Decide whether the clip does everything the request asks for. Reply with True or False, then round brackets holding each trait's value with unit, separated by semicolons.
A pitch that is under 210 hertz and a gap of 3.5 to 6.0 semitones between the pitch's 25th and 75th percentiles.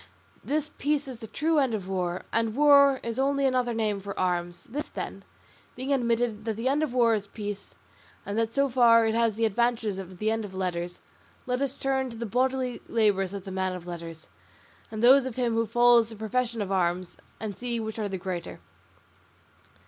False (225 Hz; 4.3 semitones)